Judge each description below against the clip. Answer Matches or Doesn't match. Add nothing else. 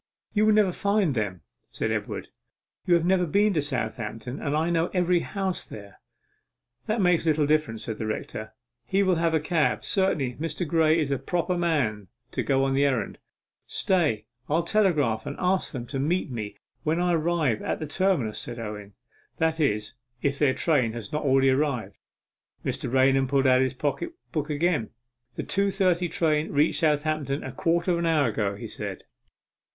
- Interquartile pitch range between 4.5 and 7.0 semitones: Matches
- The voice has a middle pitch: Matches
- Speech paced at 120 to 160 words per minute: Doesn't match